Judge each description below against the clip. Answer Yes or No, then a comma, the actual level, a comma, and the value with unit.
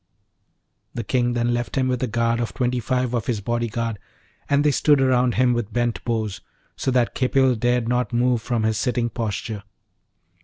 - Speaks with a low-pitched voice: Yes, low, 120 Hz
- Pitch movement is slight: Yes, narrow, 1.4 semitones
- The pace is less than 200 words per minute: Yes, average, 190 wpm